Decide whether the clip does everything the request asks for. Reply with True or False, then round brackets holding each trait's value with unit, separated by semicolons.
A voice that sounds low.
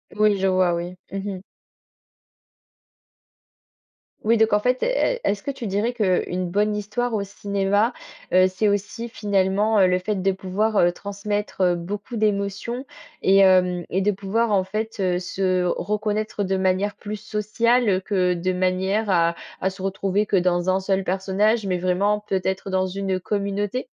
False (195 Hz)